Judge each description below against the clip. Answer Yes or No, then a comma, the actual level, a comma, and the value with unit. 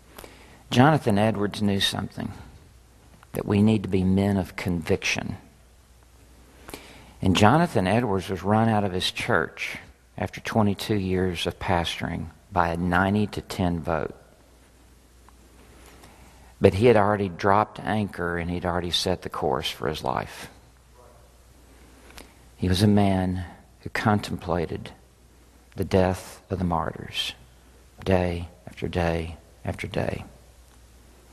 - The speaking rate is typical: No, slow, 120 wpm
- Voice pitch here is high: No, very low, 90 Hz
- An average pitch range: No, wide, 6.5 semitones